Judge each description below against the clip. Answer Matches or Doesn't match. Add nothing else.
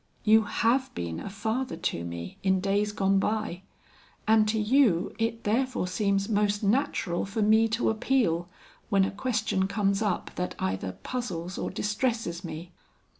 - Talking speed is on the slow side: Doesn't match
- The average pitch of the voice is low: Doesn't match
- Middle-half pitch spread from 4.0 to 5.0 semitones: Doesn't match